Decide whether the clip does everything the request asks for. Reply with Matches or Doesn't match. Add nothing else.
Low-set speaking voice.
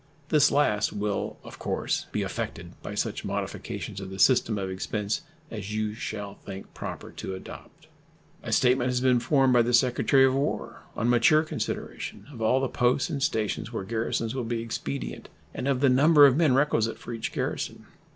Matches